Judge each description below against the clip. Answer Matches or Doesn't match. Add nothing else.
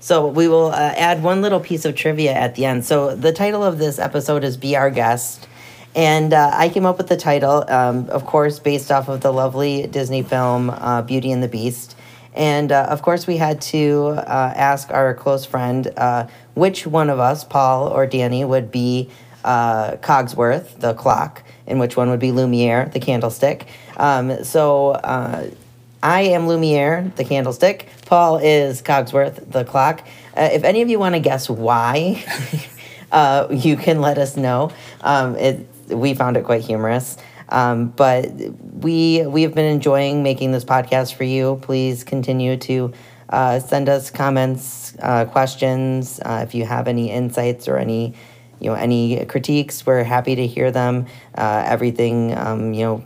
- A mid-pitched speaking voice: Doesn't match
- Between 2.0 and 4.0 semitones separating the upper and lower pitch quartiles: Matches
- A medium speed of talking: Matches